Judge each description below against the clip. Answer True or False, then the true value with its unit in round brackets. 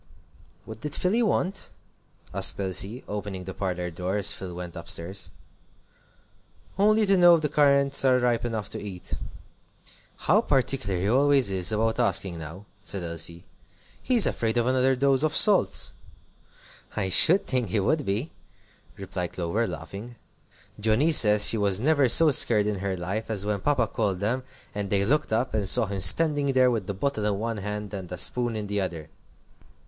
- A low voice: True (105 Hz)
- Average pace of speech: True (175 wpm)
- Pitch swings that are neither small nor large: False (5.7 semitones)